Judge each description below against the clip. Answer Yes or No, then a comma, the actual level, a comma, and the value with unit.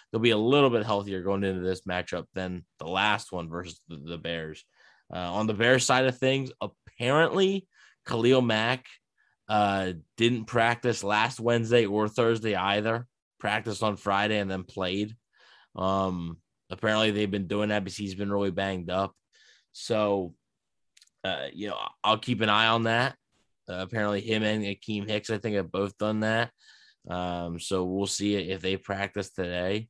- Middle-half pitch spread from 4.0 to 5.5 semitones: No, average, 3.1 semitones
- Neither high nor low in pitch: No, low, 105 Hz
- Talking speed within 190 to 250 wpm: No, average, 165 wpm